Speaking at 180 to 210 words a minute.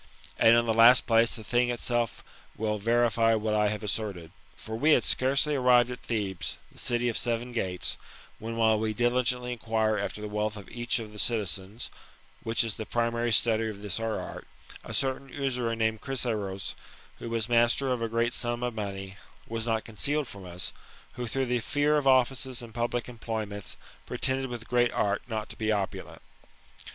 Yes: average, 190 wpm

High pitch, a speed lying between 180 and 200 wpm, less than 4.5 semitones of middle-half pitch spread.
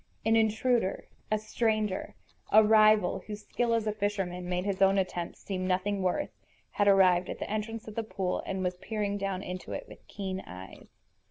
Yes: high, 200 Hz; average, 185 wpm; narrow, 2.6 semitones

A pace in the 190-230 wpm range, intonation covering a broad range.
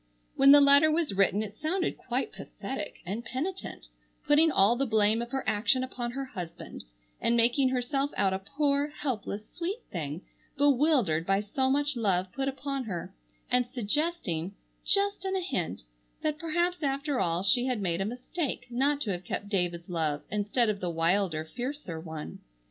No: average, 170 wpm; wide, 6.7 semitones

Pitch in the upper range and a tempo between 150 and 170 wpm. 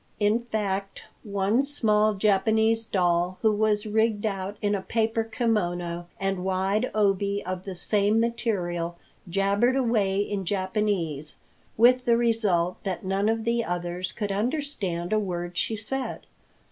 No: high, 205 Hz; average, 140 wpm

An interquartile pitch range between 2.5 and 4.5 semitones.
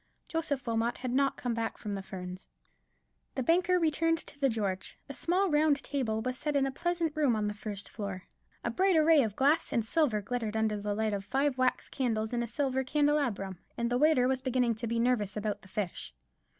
No: wide, 5.4 semitones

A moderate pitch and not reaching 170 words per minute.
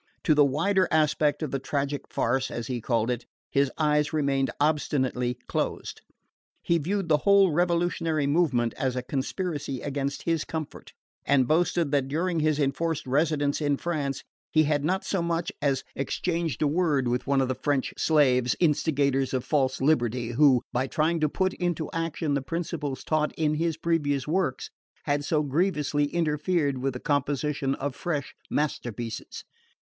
Yes: medium, 145 Hz; average, 160 wpm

